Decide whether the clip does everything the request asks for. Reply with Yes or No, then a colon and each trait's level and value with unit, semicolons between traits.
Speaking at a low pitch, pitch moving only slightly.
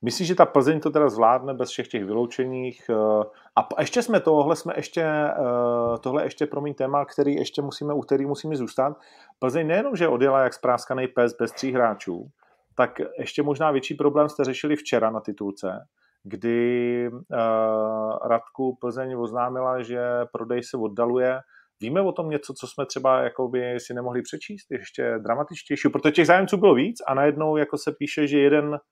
No: low, 130 Hz; average, 3.6 semitones